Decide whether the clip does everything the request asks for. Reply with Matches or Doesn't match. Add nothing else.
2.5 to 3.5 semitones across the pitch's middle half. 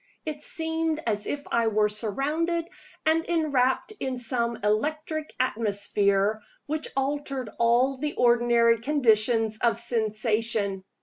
Doesn't match